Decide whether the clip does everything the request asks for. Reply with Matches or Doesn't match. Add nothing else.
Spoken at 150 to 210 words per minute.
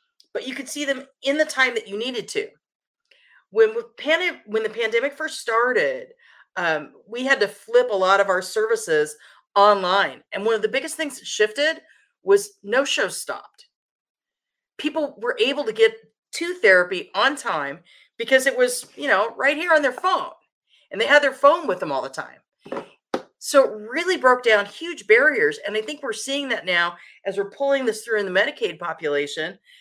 Matches